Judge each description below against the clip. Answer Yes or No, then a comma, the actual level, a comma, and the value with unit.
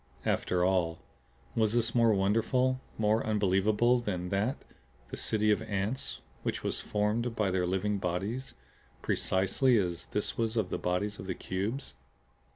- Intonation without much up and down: No, average, 3.4 semitones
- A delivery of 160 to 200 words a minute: No, average, 150 wpm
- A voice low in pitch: Yes, low, 105 Hz